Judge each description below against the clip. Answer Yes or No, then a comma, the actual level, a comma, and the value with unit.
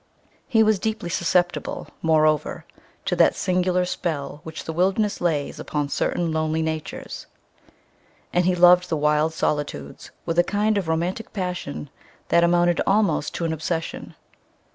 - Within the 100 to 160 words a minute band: Yes, average, 140 wpm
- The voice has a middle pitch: Yes, medium, 170 Hz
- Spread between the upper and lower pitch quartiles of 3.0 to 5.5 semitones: No, narrow, 2.5 semitones